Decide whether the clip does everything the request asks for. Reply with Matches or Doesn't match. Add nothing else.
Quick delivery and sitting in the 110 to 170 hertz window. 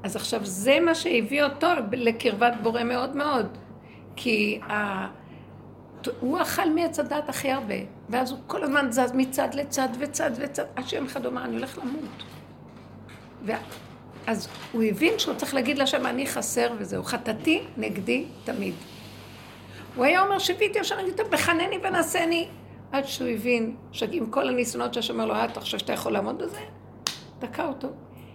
Doesn't match